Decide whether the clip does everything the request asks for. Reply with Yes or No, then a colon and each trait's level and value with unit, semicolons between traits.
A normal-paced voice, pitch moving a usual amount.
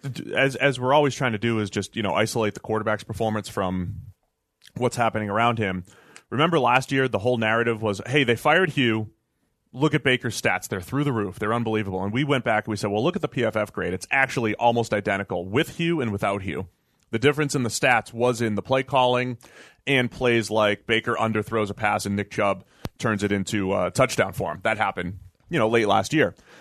No: fast, 220 wpm; average, 3.4 semitones